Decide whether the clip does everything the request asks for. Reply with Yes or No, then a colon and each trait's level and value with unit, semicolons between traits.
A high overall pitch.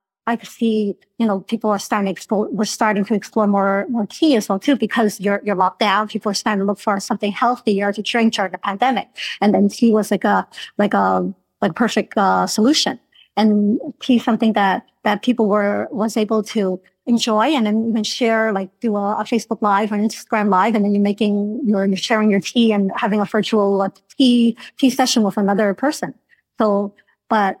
Yes: high, 215 Hz